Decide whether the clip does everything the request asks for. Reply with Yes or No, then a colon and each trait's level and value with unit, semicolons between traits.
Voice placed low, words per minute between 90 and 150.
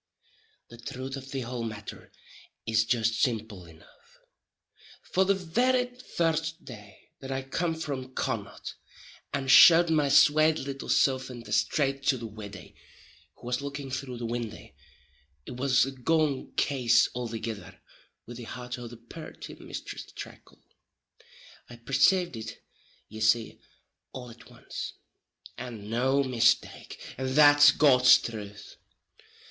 Yes: low, 130 Hz; slow, 135 wpm